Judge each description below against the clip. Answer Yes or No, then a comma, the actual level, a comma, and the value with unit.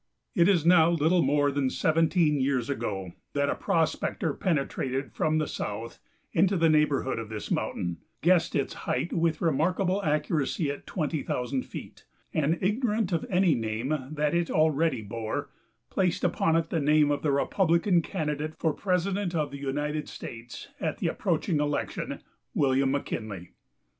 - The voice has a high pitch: No, medium, 150 Hz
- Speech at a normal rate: Yes, average, 155 wpm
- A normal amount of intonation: Yes, average, 3.6 semitones